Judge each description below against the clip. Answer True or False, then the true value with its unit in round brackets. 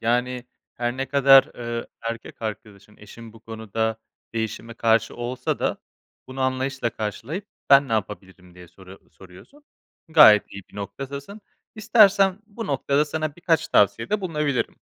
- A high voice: False (120 Hz)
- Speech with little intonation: False (4.9 semitones)